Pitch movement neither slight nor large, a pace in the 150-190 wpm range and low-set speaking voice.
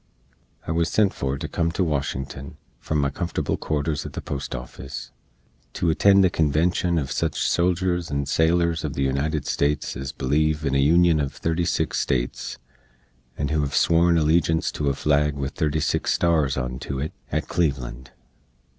Yes: average, 3.4 semitones; average, 165 wpm; very low, 75 Hz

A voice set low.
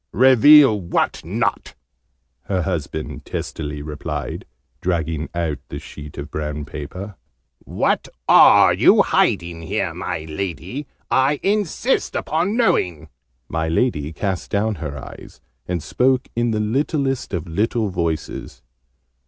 Yes: very low, 90 Hz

